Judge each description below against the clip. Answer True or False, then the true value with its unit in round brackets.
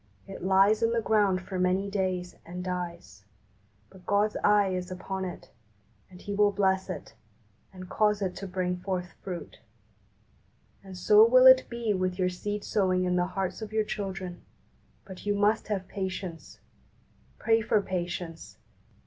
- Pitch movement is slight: True (2.2 semitones)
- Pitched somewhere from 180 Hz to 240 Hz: True (190 Hz)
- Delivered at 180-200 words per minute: False (160 wpm)